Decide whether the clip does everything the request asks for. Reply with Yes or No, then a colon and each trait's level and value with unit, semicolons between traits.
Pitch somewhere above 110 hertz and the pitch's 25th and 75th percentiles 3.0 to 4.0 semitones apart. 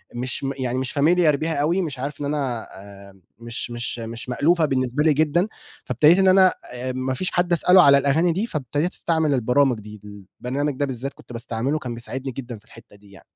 No: low, 135 Hz; average, 4.4 semitones